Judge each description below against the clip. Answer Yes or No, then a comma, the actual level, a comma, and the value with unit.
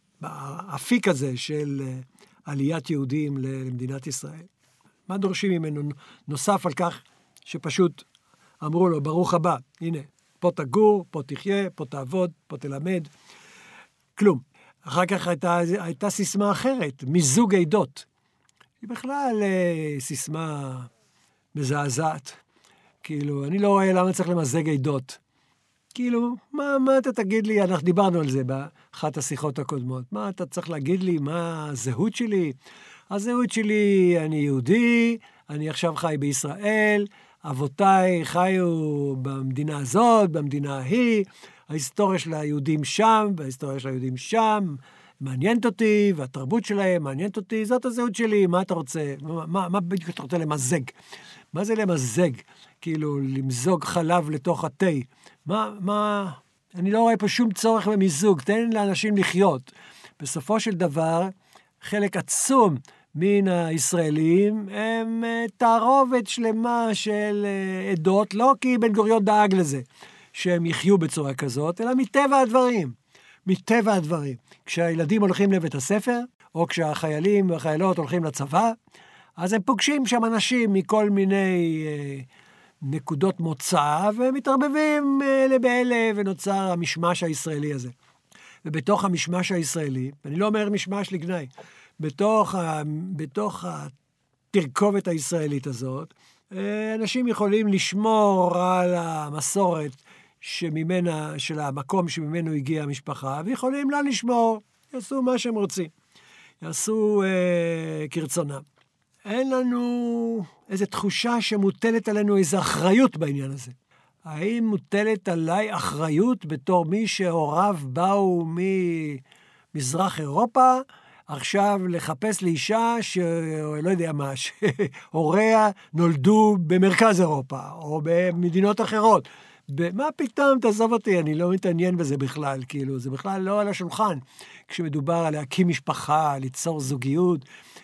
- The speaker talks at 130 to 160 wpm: No, average, 120 wpm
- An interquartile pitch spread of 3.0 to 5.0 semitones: No, wide, 5.5 semitones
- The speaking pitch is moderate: Yes, medium, 180 Hz